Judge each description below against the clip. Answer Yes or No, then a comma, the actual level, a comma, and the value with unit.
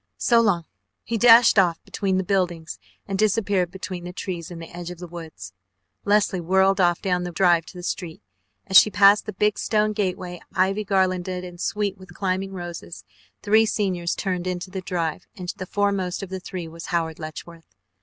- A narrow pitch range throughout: Yes, narrow, 2.3 semitones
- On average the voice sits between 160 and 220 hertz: Yes, medium, 185 Hz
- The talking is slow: No, average, 190 wpm